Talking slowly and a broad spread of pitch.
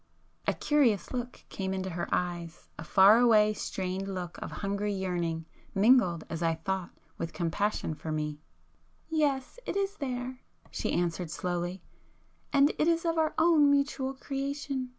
No: average, 145 wpm; wide, 7.6 semitones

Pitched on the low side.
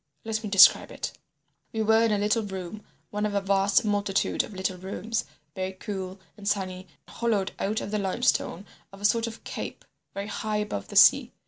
No: high, 205 Hz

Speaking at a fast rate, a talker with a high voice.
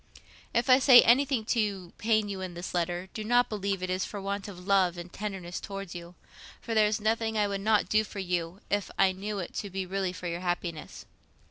Yes: fast, 225 wpm; high, 195 Hz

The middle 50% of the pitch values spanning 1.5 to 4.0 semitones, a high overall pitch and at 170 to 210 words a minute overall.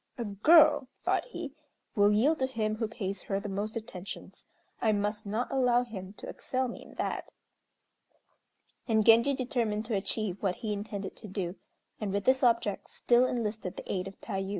Yes: average, 3.3 semitones; high, 215 Hz; average, 180 wpm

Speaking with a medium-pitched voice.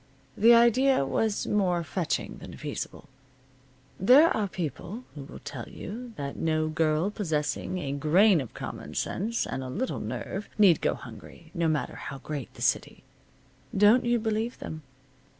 Yes: medium, 180 Hz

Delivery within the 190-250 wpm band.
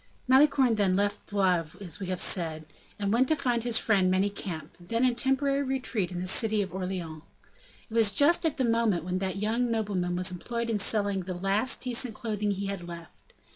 Yes: average, 200 wpm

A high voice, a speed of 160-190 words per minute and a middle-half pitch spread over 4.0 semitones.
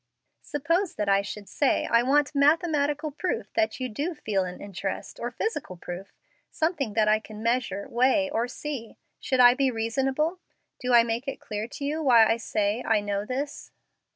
Yes: high, 245 Hz; average, 180 wpm; average, 5.2 semitones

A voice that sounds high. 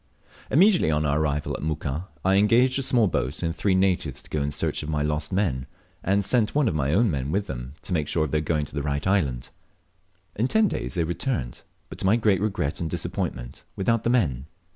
No: very low, 80 Hz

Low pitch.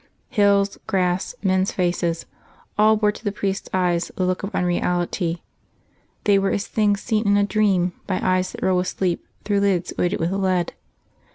No: high, 190 Hz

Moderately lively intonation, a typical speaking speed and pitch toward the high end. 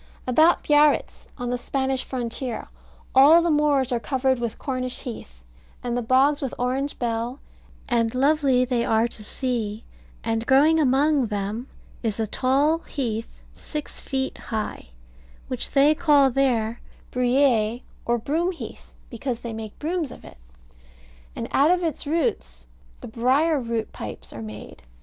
Yes: average, 3.7 semitones; average, 145 wpm; very high, 255 Hz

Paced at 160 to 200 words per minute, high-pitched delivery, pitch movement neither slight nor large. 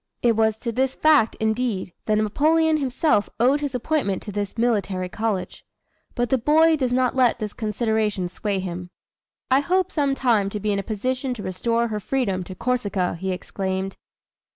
Yes: average, 175 wpm; high, 225 Hz; average, 4.5 semitones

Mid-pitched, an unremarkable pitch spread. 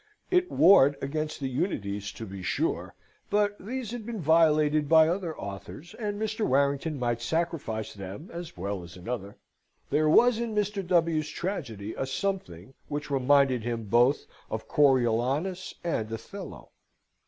No: medium, 150 Hz; wide, 7.5 semitones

